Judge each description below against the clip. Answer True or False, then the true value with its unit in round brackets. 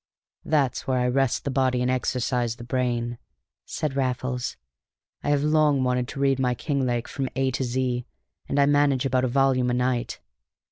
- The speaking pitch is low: True (130 Hz)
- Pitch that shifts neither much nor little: False (1.7 semitones)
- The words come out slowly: False (180 wpm)